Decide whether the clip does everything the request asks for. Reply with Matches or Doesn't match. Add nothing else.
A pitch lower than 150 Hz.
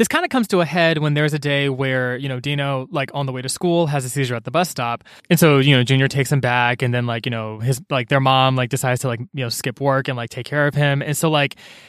Matches